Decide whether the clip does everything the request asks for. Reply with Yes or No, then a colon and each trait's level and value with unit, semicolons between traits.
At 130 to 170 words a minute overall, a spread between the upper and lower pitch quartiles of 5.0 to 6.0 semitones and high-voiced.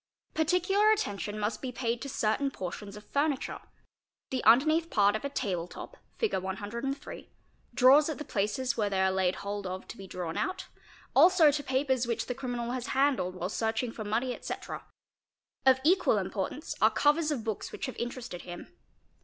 No: average, 185 wpm; wide, 5.5 semitones; high, 240 Hz